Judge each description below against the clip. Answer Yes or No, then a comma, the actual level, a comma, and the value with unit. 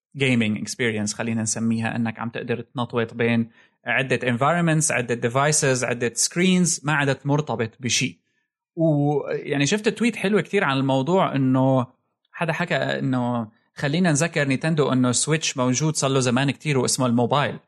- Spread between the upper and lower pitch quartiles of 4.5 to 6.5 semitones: Yes, average, 4.8 semitones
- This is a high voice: No, low, 135 Hz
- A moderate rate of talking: No, fast, 145 wpm